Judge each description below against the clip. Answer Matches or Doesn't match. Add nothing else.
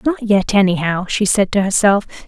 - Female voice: Matches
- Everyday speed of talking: Matches